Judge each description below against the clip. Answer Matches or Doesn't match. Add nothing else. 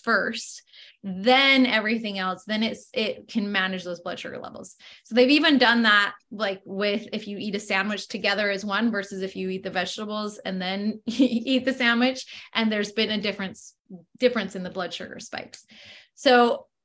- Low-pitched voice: Doesn't match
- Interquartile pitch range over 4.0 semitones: Doesn't match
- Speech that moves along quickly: Doesn't match